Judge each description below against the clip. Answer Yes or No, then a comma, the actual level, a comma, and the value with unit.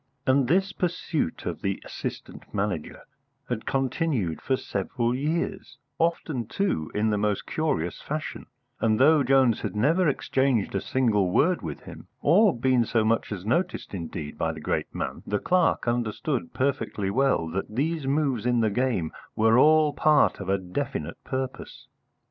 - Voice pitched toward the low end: Yes, low, 125 Hz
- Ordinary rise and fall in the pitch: No, wide, 6.2 semitones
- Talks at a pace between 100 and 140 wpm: No, average, 160 wpm